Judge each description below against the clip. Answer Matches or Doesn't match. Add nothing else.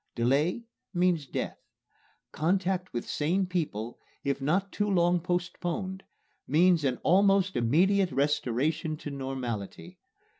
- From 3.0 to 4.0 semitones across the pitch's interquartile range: Doesn't match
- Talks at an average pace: Doesn't match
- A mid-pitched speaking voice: Matches